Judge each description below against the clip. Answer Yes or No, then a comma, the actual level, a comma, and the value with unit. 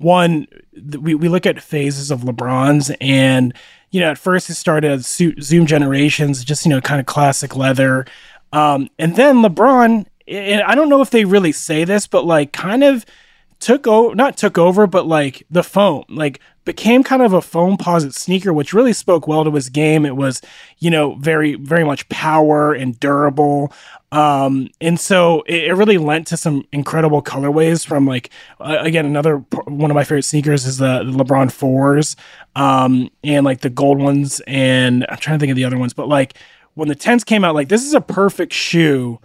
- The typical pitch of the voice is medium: Yes, medium, 150 Hz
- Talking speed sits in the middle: Yes, average, 195 wpm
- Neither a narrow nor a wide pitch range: Yes, average, 4.0 semitones